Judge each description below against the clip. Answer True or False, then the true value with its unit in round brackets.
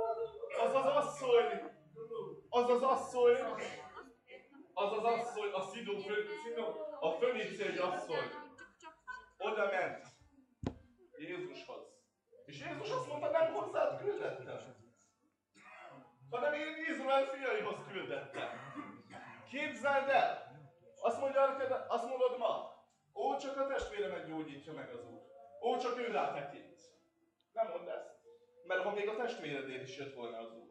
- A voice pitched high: True (265 Hz)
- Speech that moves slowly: False (125 wpm)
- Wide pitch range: True (7.4 semitones)